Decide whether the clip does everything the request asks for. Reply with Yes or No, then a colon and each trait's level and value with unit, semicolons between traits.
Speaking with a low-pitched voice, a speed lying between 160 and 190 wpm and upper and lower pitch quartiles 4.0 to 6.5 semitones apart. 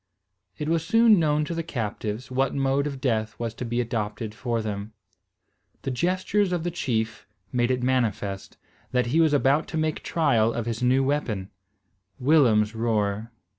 Yes: low, 125 Hz; average, 170 wpm; average, 5.2 semitones